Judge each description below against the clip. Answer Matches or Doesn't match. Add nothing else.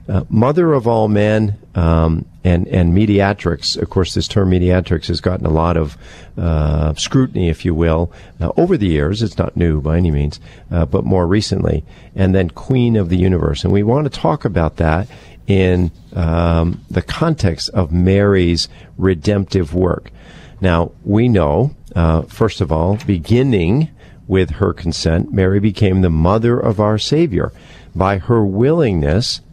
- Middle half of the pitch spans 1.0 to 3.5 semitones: Doesn't match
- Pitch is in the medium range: Doesn't match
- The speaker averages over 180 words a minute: Doesn't match